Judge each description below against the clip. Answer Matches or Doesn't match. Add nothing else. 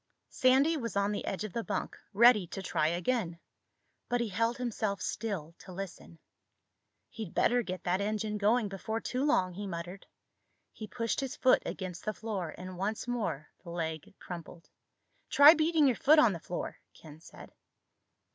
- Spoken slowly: Doesn't match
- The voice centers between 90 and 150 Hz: Doesn't match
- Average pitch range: Matches